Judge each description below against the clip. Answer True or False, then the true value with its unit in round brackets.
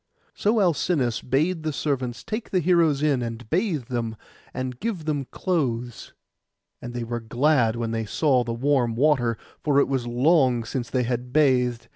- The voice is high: False (130 Hz)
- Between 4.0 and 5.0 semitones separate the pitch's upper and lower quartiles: True (4.3 semitones)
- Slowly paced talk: False (170 wpm)